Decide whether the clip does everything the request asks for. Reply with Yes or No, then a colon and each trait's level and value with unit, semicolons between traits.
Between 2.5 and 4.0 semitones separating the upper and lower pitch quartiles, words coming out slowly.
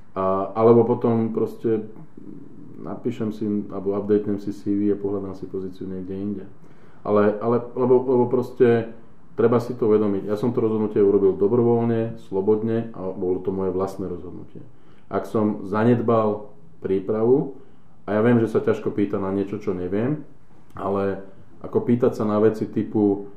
No: average, 2.9 semitones; average, 150 wpm